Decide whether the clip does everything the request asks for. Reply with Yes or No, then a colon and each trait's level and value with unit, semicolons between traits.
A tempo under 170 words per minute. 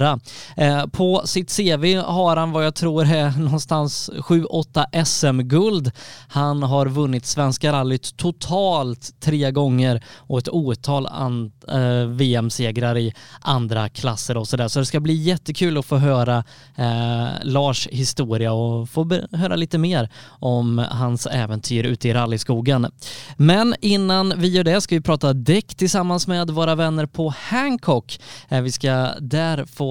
Yes: average, 140 wpm